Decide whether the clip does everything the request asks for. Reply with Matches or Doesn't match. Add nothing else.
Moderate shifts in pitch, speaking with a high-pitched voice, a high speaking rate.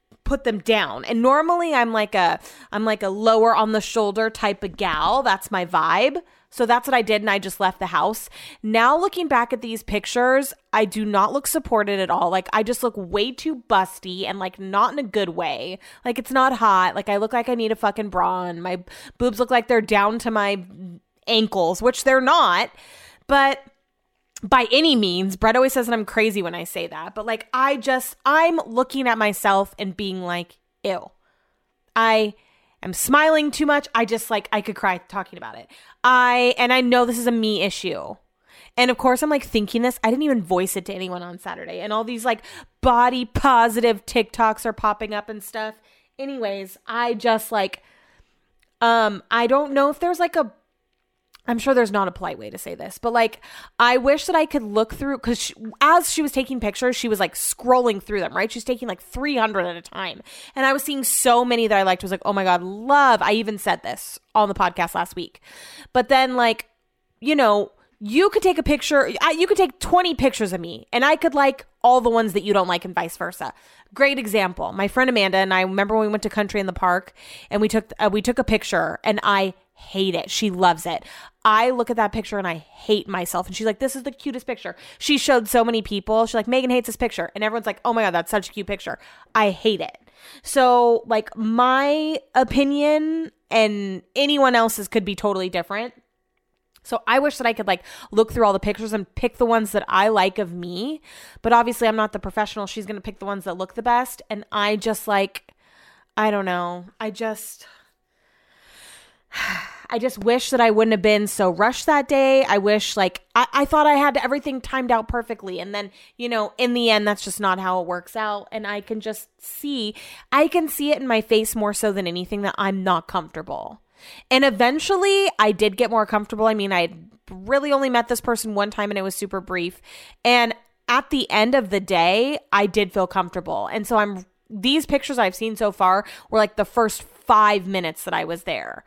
Matches